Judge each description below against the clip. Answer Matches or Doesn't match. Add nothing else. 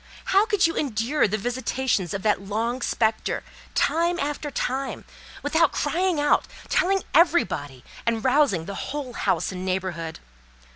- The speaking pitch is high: Matches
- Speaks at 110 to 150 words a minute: Matches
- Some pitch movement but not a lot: Doesn't match